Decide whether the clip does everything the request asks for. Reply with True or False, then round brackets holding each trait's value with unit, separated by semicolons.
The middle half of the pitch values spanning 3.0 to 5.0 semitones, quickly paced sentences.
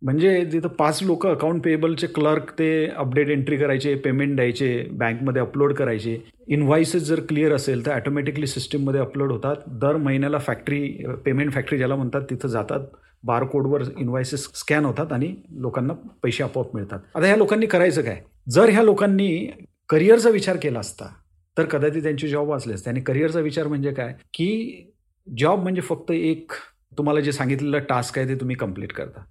True (3.4 semitones; 165 wpm)